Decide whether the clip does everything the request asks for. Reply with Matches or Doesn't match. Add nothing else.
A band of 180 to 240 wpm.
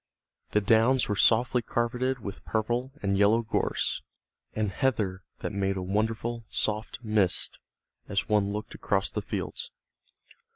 Doesn't match